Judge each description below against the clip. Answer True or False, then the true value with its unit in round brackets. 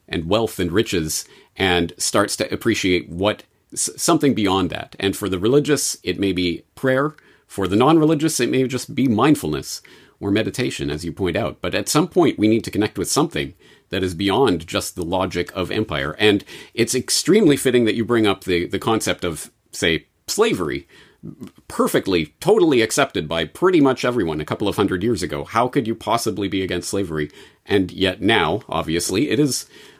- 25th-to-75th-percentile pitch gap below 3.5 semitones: False (4.5 semitones)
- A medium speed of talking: True (185 wpm)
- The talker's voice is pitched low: True (100 Hz)